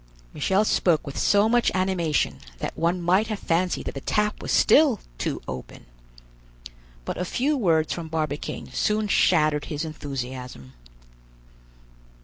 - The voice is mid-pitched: Yes, medium, 170 Hz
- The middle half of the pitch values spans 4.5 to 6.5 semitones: Yes, wide, 5.5 semitones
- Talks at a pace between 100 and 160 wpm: Yes, slow, 135 wpm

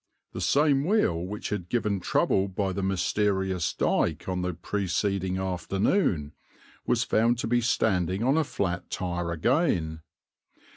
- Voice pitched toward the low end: Yes, very low, 95 Hz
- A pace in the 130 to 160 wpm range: Yes, average, 140 wpm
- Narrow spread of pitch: No, average, 4.3 semitones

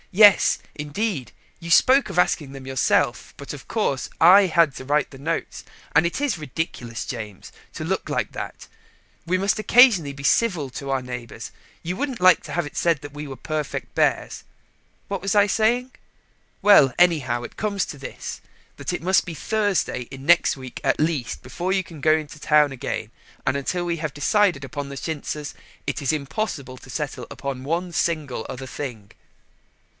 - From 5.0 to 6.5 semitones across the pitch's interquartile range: Yes, average, 5.3 semitones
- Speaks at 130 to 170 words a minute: No, average, 180 wpm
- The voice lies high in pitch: No, medium, 155 Hz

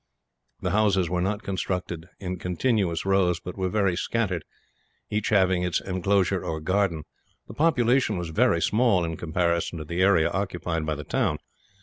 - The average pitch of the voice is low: Yes, very low, 90 Hz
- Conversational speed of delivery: Yes, average, 165 wpm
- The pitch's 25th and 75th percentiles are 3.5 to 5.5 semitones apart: No, average, 2.9 semitones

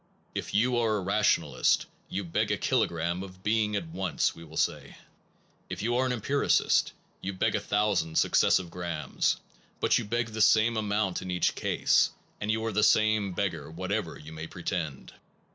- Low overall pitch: Yes, low, 100 Hz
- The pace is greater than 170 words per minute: Yes, average, 180 wpm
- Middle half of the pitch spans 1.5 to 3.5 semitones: No, average, 4.0 semitones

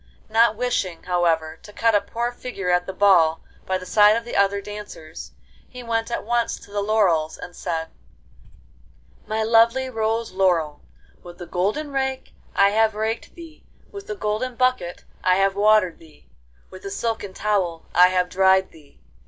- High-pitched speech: Yes, high, 205 Hz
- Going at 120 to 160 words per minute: No, average, 170 wpm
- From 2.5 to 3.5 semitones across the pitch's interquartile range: No, average, 4.0 semitones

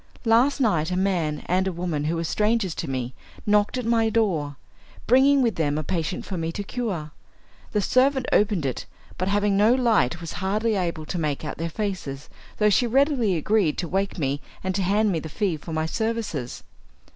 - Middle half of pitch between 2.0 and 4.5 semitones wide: No, wide, 5.6 semitones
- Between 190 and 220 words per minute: Yes, average, 200 wpm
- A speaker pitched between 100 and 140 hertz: No, high, 190 Hz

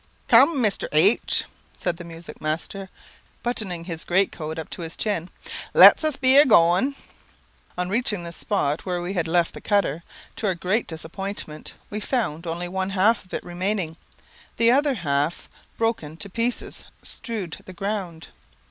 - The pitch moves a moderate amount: Yes, average, 4.4 semitones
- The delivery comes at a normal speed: Yes, average, 165 wpm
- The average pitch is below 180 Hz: No, medium, 185 Hz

